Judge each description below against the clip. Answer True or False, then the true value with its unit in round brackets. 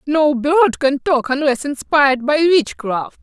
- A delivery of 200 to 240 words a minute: False (150 wpm)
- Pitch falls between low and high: False (285 Hz)